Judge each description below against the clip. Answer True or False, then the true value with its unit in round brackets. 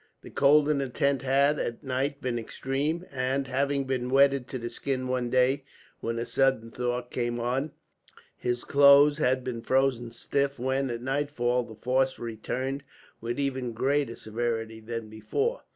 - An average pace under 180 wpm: True (165 wpm)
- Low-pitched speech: True (130 Hz)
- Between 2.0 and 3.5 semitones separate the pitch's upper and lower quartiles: True (2.5 semitones)